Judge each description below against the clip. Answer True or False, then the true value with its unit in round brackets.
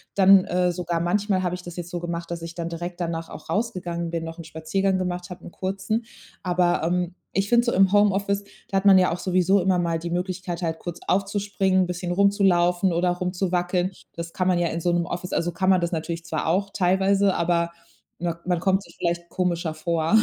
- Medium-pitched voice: True (180 Hz)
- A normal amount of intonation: False (1.9 semitones)